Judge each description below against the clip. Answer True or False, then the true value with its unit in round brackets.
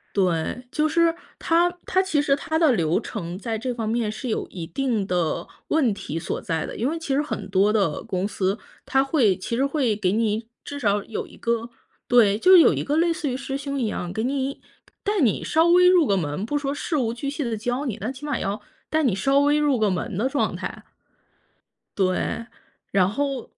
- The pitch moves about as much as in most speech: False (6.1 semitones)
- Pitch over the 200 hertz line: True (245 Hz)